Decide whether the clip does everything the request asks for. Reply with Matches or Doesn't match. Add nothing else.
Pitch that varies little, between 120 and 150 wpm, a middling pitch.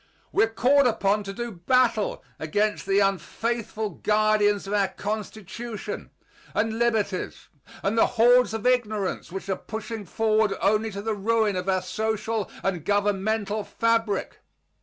Doesn't match